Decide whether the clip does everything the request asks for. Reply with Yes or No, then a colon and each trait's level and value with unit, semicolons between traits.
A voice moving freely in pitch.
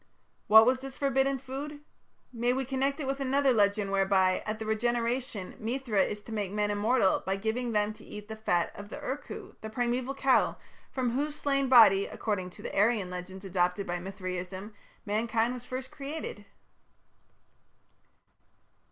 No: average, 4.6 semitones